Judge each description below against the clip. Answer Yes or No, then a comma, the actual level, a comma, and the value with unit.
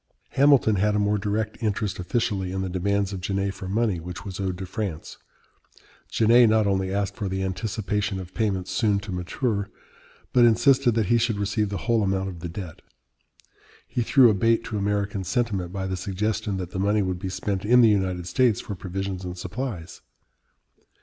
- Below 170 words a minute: No, average, 190 wpm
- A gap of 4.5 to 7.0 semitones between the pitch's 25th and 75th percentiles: No, average, 2.7 semitones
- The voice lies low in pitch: Yes, low, 100 Hz